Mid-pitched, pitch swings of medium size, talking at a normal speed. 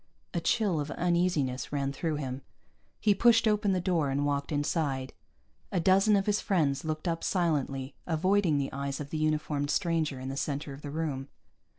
Yes: medium, 155 Hz; average, 4.2 semitones; average, 185 wpm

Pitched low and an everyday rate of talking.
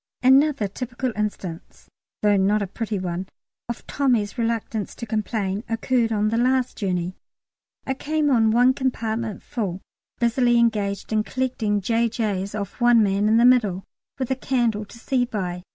No: high, 225 Hz; average, 155 wpm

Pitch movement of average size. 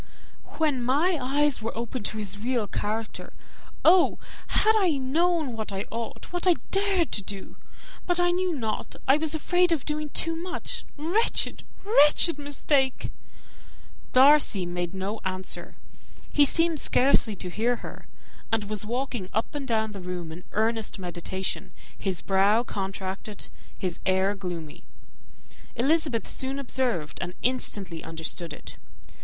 No: wide, 7.5 semitones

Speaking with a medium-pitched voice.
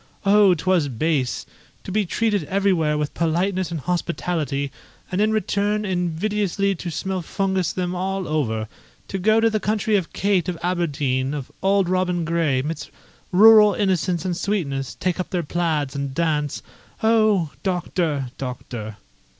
Yes: medium, 180 Hz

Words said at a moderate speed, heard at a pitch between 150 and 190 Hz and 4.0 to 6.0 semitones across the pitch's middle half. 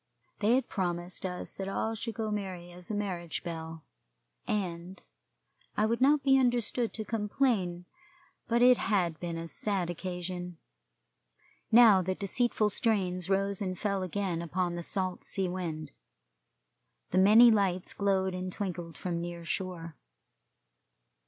No: average, 145 wpm; medium, 185 Hz; average, 3.3 semitones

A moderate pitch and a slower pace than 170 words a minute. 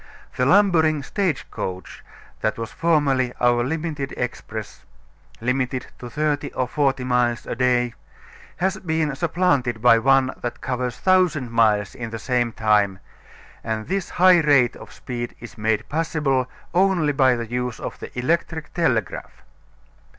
No: low, 130 Hz; average, 145 wpm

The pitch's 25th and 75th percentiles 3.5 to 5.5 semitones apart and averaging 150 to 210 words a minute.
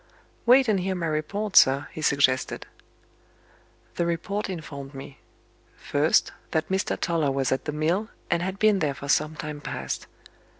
Yes: average, 5.1 semitones; average, 160 wpm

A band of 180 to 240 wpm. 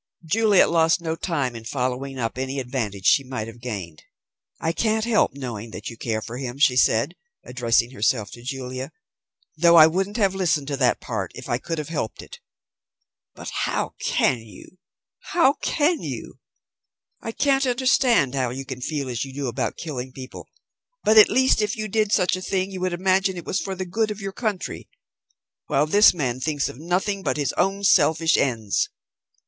Yes: average, 190 wpm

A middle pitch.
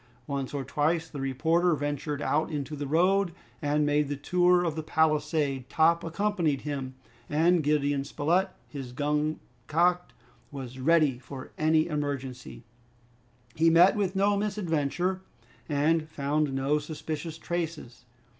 Yes: medium, 150 Hz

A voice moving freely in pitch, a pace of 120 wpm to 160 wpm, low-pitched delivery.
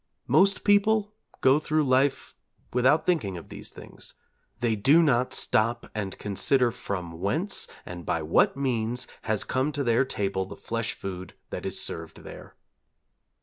Yes: wide, 6.5 semitones; average, 150 wpm; low, 120 Hz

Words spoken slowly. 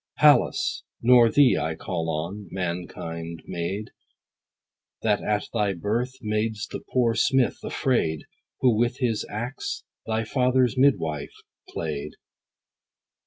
Yes: slow, 115 wpm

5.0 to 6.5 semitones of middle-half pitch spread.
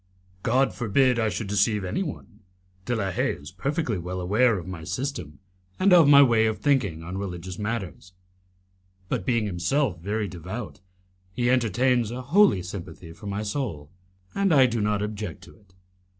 Yes: wide, 5.4 semitones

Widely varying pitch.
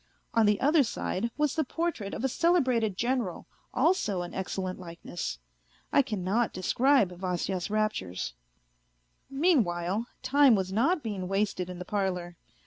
Yes: wide, 6.3 semitones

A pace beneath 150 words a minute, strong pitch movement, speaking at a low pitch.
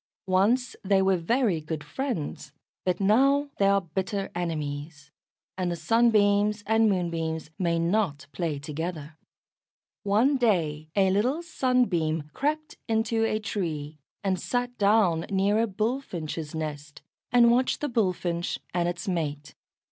No: slow, 135 wpm; wide, 5.7 semitones; high, 190 Hz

